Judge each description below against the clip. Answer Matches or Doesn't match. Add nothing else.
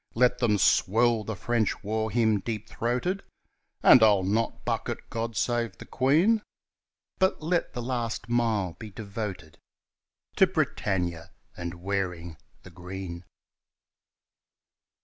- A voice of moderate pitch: Doesn't match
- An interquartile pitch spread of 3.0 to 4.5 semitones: Matches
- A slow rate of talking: Matches